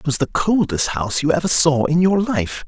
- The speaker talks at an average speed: No, fast, 245 wpm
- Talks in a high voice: No, medium, 155 Hz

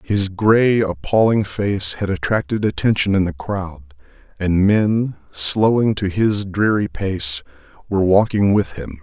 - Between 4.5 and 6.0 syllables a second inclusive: No, 4.0 syllables/s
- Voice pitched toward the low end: Yes, very low, 95 Hz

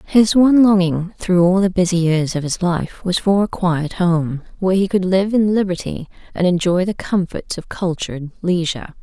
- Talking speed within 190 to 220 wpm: Yes, average, 195 wpm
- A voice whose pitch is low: No, medium, 180 Hz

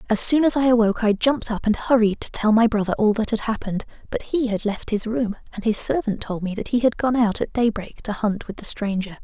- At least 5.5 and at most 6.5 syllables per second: Yes, 6.0 syllables/s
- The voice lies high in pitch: Yes, high, 220 Hz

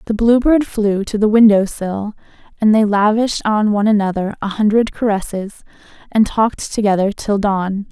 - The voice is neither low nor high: No, high, 210 Hz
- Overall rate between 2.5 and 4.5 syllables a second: No, 5.2 syllables/s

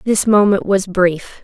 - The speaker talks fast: No, average, 165 wpm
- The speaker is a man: No, female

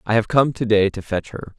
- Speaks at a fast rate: Yes, fast, 305 wpm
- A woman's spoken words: No, male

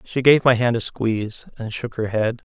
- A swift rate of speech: Yes, fast, 240 wpm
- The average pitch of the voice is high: No, low, 115 Hz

